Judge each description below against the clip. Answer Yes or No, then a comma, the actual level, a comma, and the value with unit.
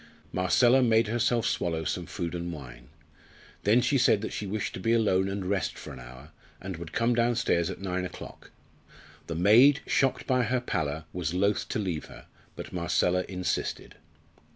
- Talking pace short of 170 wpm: No, average, 175 wpm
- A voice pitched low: Yes, very low, 95 Hz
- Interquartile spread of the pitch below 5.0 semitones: No, average, 5.3 semitones